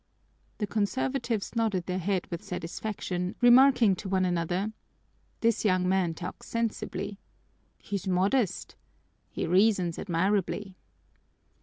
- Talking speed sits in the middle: No, slow, 110 wpm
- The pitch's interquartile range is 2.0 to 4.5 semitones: Yes, average, 3.3 semitones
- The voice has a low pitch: No, high, 195 Hz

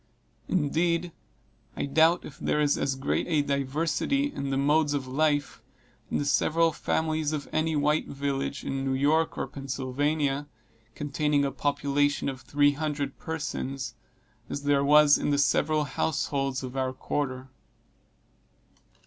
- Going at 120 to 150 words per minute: Yes, average, 140 wpm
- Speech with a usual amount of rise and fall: No, narrow, 2.0 semitones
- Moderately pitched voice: Yes, medium, 145 Hz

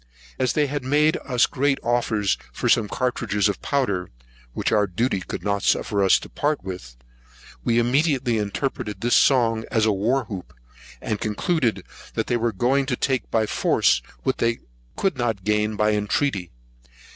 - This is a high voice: No, low, 115 Hz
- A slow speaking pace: No, average, 170 wpm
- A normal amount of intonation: Yes, average, 4.1 semitones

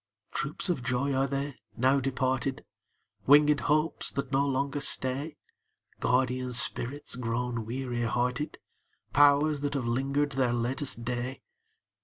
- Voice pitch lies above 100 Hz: Yes, low, 135 Hz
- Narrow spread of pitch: Yes, narrow, 2.3 semitones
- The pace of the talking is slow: Yes, slow, 125 wpm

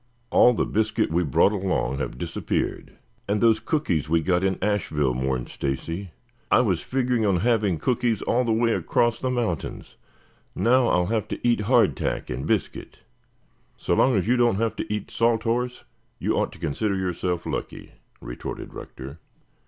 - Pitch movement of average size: No, wide, 5.9 semitones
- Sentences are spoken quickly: No, average, 170 wpm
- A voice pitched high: No, low, 105 Hz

